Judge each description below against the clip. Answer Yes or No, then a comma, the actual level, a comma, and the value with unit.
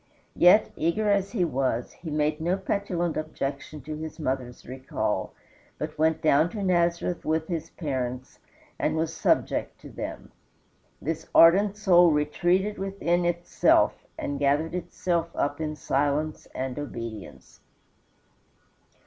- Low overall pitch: No, medium, 160 Hz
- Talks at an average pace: No, slow, 130 wpm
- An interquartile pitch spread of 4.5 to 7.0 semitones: No, average, 3.4 semitones